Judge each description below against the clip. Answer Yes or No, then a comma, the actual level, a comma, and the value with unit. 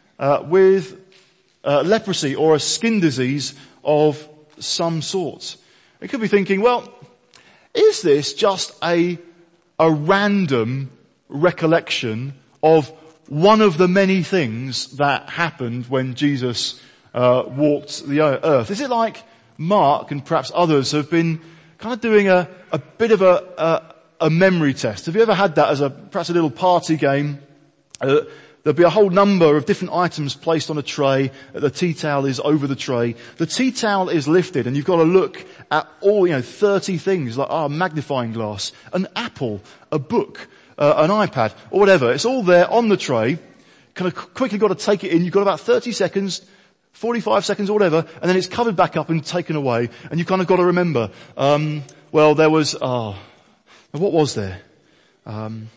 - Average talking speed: Yes, average, 180 wpm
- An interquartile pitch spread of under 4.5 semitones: No, average, 5.0 semitones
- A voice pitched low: No, medium, 165 Hz